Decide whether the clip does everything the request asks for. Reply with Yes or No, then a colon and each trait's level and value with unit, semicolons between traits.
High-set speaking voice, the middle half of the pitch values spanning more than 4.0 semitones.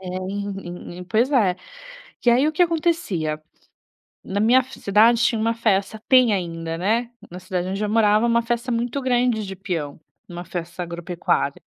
Yes: high, 210 Hz; average, 4.8 semitones